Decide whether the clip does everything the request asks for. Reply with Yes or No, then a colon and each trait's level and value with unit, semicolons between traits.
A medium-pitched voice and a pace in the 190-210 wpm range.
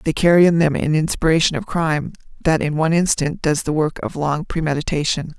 Yes: medium, 155 Hz; average, 200 wpm